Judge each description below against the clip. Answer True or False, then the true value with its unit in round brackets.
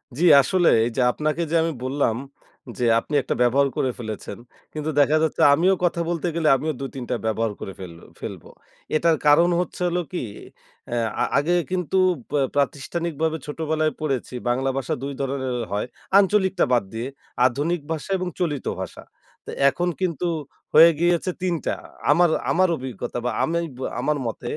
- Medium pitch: True (150 Hz)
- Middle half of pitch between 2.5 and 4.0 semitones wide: False (4.7 semitones)